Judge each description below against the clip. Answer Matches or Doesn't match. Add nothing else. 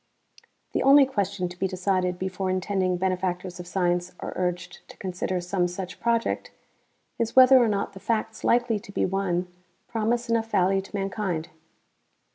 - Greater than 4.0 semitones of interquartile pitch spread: Doesn't match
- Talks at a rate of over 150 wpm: Matches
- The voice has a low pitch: Doesn't match